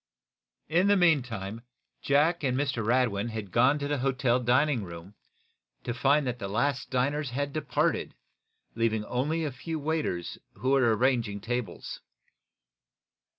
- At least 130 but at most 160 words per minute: Yes, average, 140 wpm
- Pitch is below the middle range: Yes, low, 130 Hz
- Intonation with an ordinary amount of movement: Yes, average, 4.0 semitones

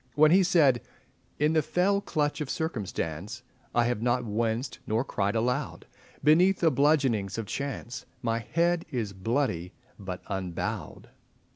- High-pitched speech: No, low, 125 Hz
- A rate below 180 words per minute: Yes, average, 140 wpm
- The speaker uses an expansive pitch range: Yes, wide, 6.3 semitones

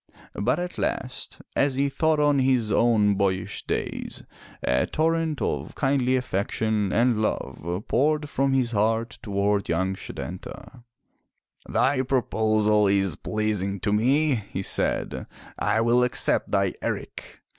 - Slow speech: Yes, slow, 130 wpm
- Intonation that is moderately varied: Yes, average, 4.7 semitones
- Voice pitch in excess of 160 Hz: No, low, 115 Hz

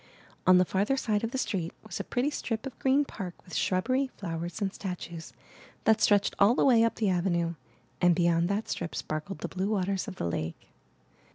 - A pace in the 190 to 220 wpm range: Yes, average, 200 wpm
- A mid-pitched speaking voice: No, high, 195 Hz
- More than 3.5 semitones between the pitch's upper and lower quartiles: Yes, average, 4.4 semitones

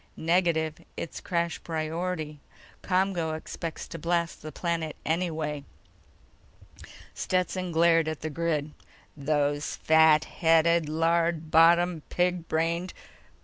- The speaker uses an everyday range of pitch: No, narrow, 1.5 semitones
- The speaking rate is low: Yes, slow, 105 wpm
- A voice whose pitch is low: No, medium, 165 Hz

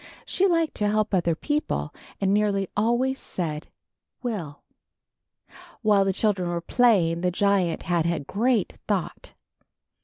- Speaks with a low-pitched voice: No, high, 200 Hz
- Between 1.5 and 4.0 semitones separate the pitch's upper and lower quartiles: No, average, 4.7 semitones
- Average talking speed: No, slow, 130 wpm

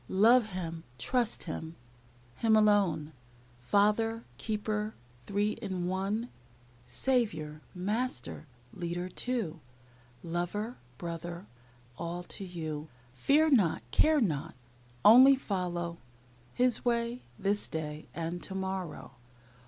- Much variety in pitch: No, average, 5.0 semitones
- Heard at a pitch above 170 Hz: Yes, high, 190 Hz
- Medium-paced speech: No, slow, 100 wpm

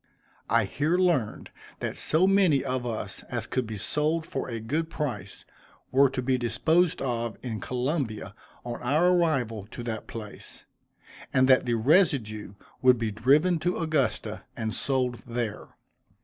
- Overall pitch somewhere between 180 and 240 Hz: No, low, 130 Hz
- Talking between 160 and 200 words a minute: No, average, 150 wpm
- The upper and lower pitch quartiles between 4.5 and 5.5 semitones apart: Yes, average, 5.2 semitones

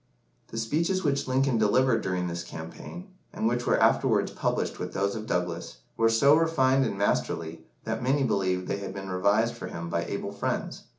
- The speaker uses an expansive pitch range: Yes, wide, 6.1 semitones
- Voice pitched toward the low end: Yes, low, 110 Hz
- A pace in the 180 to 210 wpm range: Yes, average, 185 wpm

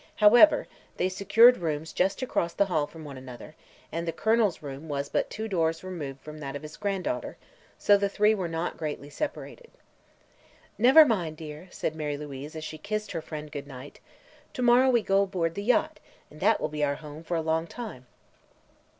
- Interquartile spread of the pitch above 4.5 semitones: Yes, wide, 5.5 semitones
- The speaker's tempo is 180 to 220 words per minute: Yes, average, 195 wpm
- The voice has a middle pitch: Yes, medium, 165 Hz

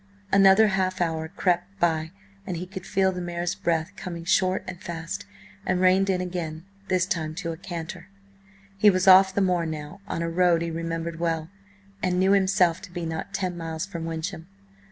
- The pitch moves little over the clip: Yes, narrow, 2.3 semitones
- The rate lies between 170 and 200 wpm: Yes, average, 190 wpm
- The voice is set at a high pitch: No, medium, 175 Hz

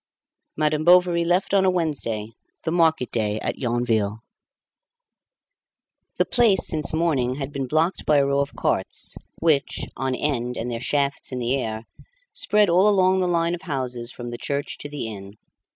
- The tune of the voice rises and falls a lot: Yes, wide, 5.7 semitones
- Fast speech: No, average, 170 wpm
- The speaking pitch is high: No, medium, 140 Hz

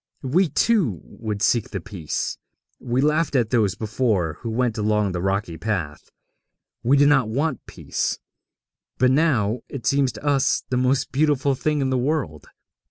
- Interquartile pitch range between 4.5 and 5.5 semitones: Yes, average, 4.8 semitones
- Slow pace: No, average, 165 wpm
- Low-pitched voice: Yes, low, 125 Hz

